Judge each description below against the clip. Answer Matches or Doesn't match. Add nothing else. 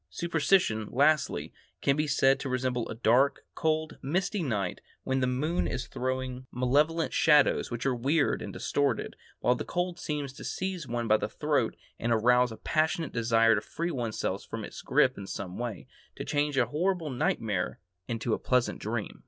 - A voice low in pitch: Matches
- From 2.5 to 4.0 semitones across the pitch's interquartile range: Doesn't match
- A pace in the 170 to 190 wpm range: Matches